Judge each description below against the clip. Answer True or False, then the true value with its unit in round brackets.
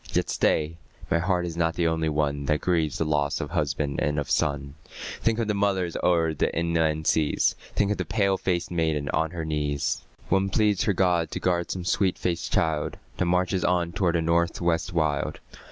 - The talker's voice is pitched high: False (85 Hz)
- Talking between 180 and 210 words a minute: True (200 wpm)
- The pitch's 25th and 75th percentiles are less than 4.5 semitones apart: True (2.8 semitones)